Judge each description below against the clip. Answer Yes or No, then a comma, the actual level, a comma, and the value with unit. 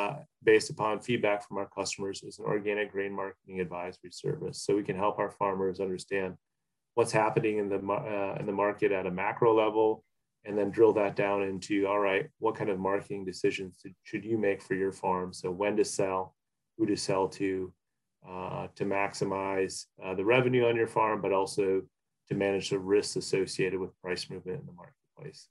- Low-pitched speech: Yes, low, 100 Hz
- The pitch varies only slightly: Yes, narrow, 1.7 semitones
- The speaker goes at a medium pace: Yes, average, 190 wpm